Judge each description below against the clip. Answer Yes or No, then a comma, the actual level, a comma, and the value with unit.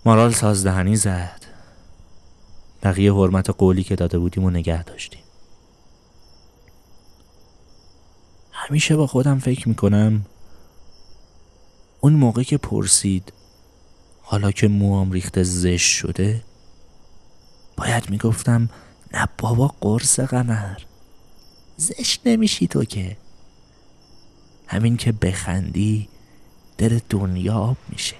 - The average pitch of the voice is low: Yes, very low, 95 Hz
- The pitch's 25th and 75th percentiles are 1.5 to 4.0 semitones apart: No, average, 4.5 semitones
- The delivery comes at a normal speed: No, slow, 95 wpm